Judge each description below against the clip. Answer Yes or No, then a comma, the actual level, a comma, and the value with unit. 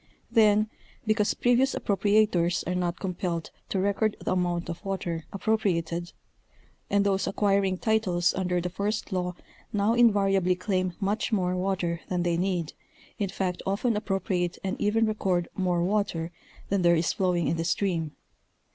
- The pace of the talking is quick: No, average, 150 wpm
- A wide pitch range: No, narrow, 2.6 semitones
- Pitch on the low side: No, high, 190 Hz